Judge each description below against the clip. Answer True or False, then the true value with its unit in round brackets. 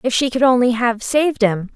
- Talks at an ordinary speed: False (240 wpm)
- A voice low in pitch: False (240 Hz)